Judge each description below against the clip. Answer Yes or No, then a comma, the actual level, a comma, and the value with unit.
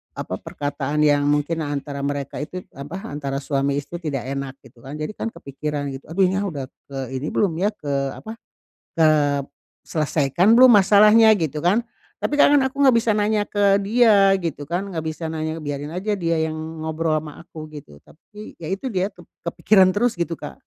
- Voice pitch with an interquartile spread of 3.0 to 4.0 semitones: No, wide, 5.5 semitones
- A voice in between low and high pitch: Yes, medium, 160 Hz